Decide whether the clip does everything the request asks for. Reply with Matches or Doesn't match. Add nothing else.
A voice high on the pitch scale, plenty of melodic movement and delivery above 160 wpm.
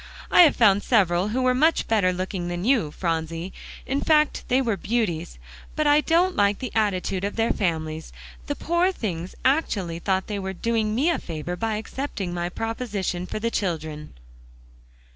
Matches